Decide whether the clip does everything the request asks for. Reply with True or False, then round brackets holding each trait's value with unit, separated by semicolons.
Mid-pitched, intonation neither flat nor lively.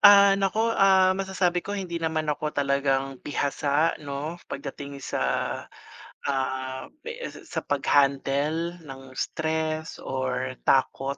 True (150 Hz; 4.3 semitones)